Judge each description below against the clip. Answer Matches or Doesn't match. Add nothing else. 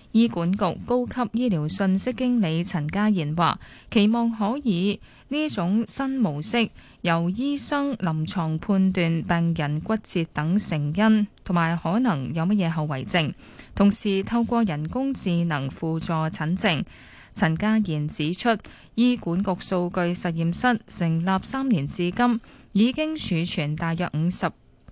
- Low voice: Doesn't match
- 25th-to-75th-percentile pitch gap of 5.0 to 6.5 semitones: Matches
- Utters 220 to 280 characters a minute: Doesn't match